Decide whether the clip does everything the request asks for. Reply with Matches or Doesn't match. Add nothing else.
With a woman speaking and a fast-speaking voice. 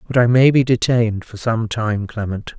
Doesn't match